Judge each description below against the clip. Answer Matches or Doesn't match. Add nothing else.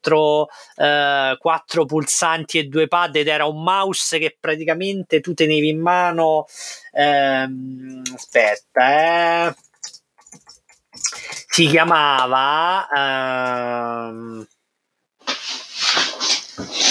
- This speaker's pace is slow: Matches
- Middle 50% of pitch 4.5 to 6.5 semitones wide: Doesn't match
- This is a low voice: Doesn't match